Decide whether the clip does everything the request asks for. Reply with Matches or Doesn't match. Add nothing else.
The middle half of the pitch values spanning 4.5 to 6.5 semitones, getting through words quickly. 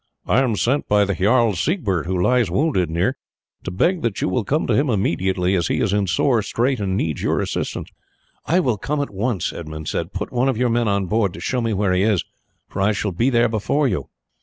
Matches